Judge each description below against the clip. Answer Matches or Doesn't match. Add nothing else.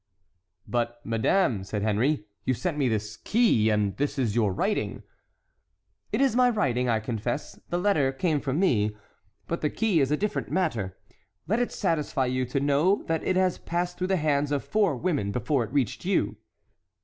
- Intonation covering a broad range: Matches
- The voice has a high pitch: Doesn't match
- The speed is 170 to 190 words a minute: Matches